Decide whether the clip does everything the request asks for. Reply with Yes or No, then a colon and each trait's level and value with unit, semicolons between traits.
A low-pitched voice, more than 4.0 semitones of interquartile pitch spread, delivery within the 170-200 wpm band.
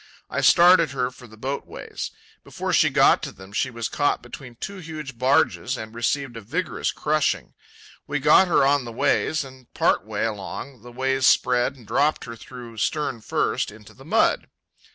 No: low, 130 Hz; average, 3.7 semitones; average, 185 wpm